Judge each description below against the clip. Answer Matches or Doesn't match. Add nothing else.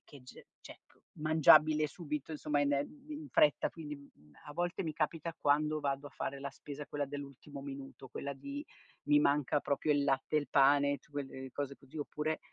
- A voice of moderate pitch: Matches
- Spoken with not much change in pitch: Matches